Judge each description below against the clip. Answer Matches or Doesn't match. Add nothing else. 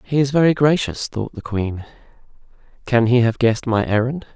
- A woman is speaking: Doesn't match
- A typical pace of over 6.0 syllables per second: Doesn't match